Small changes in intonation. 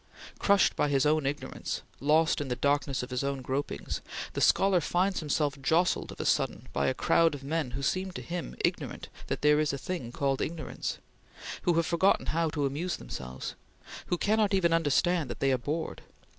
No: average, 3.8 semitones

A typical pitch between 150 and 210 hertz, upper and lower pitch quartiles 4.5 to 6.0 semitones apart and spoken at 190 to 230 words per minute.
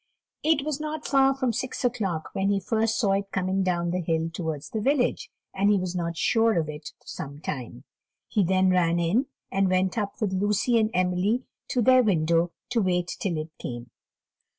Yes: high, 190 Hz; average, 5.1 semitones; average, 195 wpm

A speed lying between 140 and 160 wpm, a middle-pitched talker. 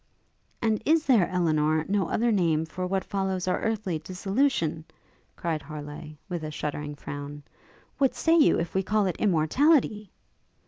Yes: average, 150 wpm; medium, 180 Hz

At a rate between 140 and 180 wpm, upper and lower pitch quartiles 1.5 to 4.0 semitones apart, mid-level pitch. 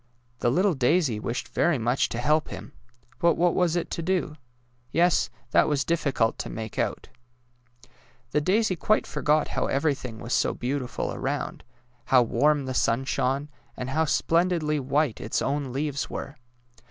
No: average, 170 wpm; average, 4.4 semitones; medium, 145 Hz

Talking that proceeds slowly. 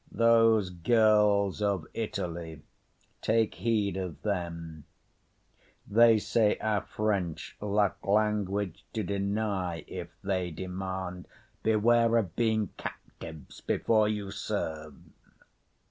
Yes: slow, 100 wpm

